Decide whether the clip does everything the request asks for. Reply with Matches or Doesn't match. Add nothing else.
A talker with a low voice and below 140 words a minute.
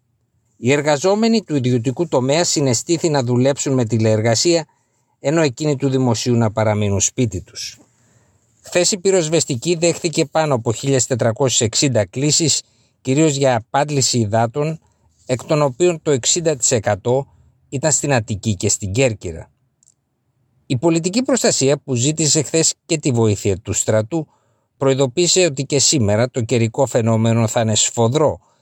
Matches